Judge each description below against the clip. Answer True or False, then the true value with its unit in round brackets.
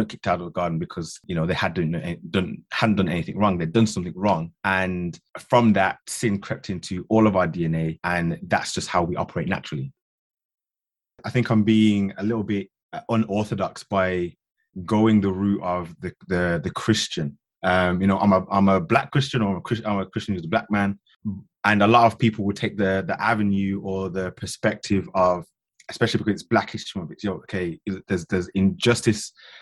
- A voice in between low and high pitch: False (100 Hz)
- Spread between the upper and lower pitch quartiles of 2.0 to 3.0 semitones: True (2.7 semitones)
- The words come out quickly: True (210 wpm)